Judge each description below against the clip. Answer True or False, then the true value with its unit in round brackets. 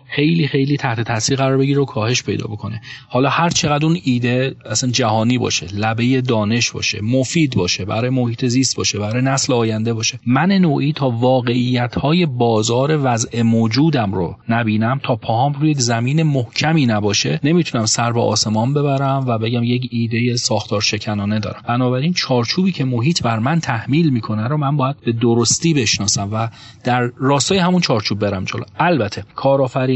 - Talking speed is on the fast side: True (160 wpm)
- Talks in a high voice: False (125 Hz)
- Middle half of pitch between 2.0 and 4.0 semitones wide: True (3.4 semitones)